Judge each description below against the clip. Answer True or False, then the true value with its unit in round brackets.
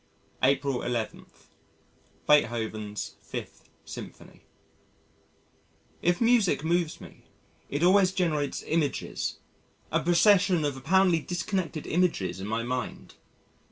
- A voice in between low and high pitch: True (155 Hz)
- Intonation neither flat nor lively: False (6.0 semitones)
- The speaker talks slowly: True (95 wpm)